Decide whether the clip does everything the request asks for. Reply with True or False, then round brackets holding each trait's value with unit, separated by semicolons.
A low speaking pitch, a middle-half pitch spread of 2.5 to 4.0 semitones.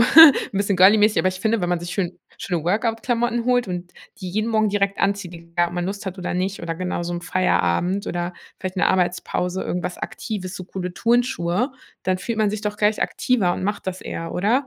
False (190 Hz; 3.3 semitones)